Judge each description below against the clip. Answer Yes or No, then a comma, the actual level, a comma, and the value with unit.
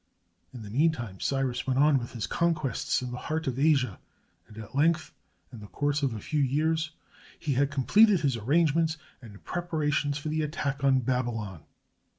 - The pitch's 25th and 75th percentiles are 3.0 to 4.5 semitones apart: Yes, average, 4.0 semitones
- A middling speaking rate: Yes, average, 185 wpm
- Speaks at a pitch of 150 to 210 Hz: No, medium, 140 Hz